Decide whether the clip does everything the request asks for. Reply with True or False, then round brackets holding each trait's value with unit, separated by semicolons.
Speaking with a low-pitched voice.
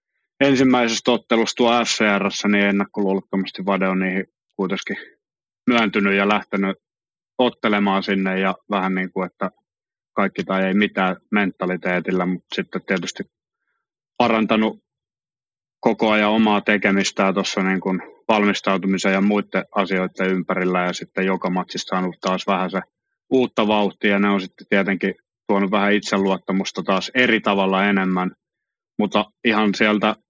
True (100 Hz)